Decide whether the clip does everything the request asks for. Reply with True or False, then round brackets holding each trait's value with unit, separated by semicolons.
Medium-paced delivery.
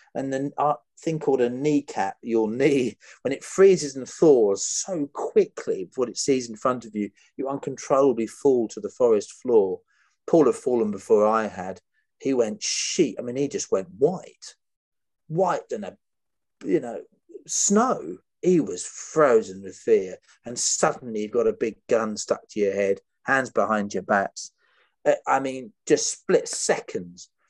True (170 wpm)